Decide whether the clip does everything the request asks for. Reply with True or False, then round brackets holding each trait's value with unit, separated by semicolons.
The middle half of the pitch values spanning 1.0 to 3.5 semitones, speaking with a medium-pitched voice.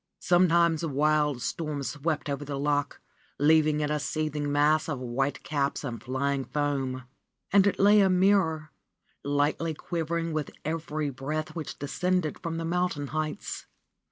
True (2.4 semitones; 150 Hz)